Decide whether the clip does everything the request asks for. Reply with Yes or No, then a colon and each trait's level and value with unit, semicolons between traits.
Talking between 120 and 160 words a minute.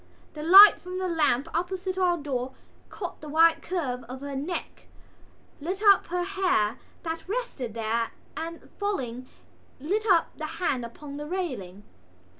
Yes: average, 150 wpm